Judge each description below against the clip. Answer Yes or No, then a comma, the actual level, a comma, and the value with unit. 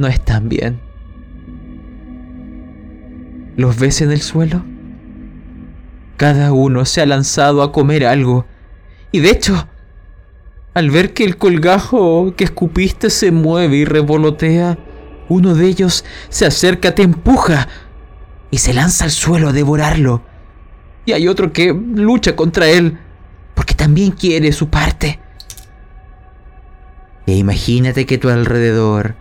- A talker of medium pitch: Yes, medium, 145 Hz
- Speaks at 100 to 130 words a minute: Yes, slow, 125 wpm